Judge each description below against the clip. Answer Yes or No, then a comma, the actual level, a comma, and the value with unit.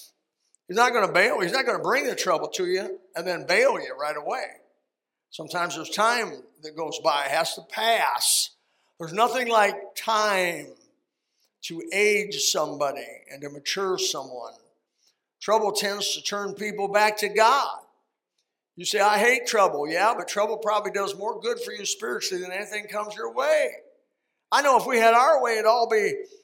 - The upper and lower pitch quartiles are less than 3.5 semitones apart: No, average, 4.3 semitones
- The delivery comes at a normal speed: Yes, average, 180 wpm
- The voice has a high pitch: Yes, high, 210 Hz